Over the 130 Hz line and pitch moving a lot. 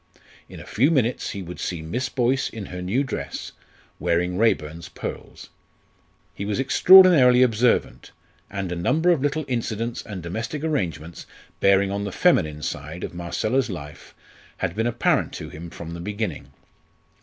No: low, 100 Hz; wide, 6.5 semitones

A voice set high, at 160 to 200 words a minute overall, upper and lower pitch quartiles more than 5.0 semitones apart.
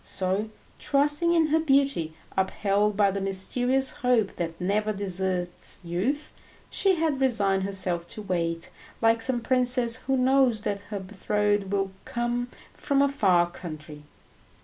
No: high, 210 Hz; average, 140 wpm; wide, 5.4 semitones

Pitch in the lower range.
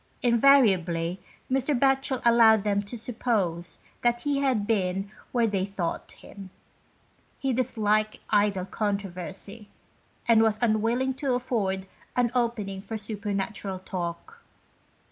No: high, 215 Hz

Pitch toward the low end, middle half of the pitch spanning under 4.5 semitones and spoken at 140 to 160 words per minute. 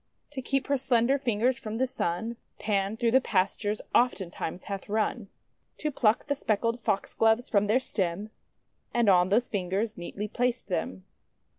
No: high, 220 Hz; average, 3.7 semitones; average, 155 wpm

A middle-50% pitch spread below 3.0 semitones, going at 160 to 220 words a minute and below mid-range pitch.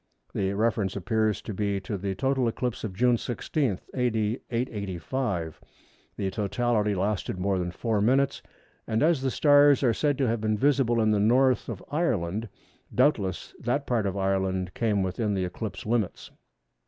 No: average, 4.2 semitones; average, 165 wpm; low, 110 Hz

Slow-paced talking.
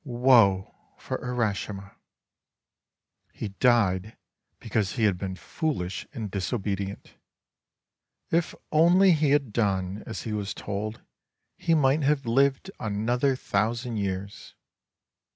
Yes: slow, 110 wpm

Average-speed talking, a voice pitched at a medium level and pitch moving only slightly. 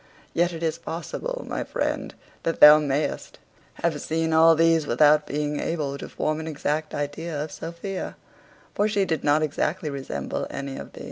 Yes: average, 175 wpm; medium, 155 Hz; narrow, 2.1 semitones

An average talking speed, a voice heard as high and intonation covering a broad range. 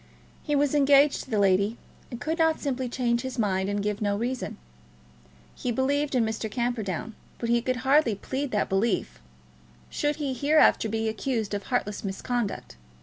No: average, 170 wpm; high, 240 Hz; average, 4.6 semitones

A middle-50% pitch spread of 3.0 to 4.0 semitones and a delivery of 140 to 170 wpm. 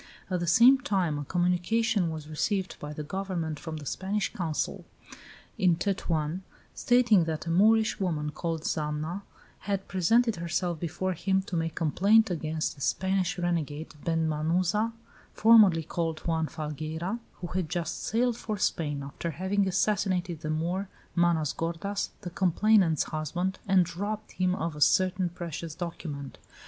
Yes: average, 3.4 semitones; average, 150 wpm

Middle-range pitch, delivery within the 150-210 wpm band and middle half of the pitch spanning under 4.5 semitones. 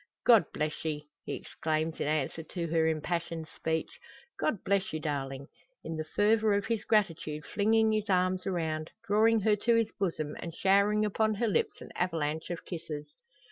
No: medium, 175 Hz; average, 175 wpm; average, 5.0 semitones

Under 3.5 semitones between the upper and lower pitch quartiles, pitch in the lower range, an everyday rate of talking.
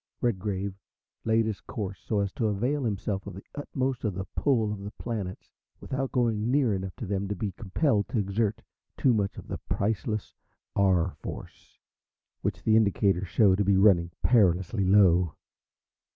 Yes: average, 2.9 semitones; low, 105 Hz; average, 165 wpm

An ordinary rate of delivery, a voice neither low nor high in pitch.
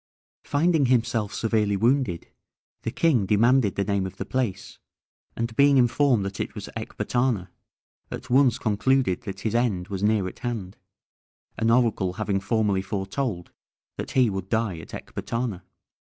No: average, 150 wpm; low, 110 Hz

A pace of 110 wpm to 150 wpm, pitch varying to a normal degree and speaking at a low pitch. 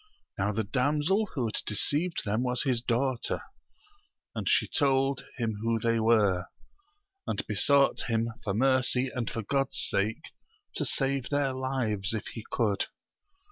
Yes: average, 145 wpm; average, 3.5 semitones; low, 125 Hz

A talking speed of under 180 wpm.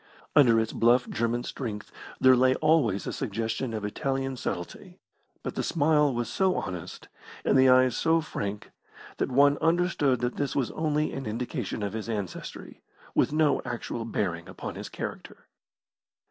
Yes: average, 160 wpm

